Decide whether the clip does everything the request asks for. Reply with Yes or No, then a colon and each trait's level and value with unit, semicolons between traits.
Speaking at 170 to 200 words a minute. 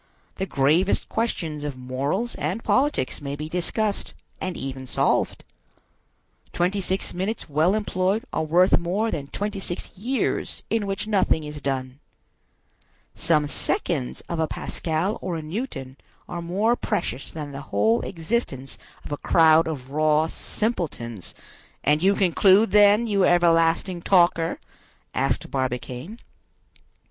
No: slow, 135 wpm